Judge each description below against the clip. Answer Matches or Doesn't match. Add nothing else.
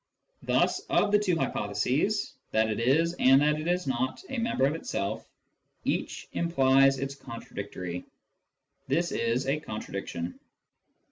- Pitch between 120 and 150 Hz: Matches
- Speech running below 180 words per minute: Matches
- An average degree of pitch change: Doesn't match